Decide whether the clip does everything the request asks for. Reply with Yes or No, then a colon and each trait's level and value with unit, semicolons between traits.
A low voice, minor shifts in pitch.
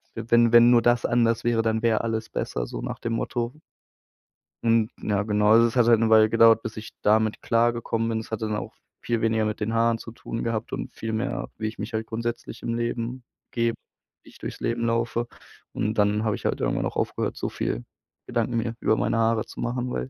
Yes: low, 115 Hz; narrow, 1.1 semitones